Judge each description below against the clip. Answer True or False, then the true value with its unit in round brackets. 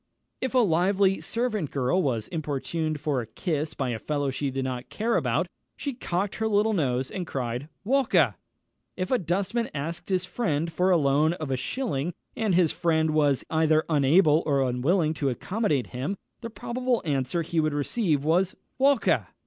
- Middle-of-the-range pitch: True (160 Hz)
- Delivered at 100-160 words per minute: False (175 wpm)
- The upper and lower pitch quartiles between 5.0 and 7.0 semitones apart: True (5.6 semitones)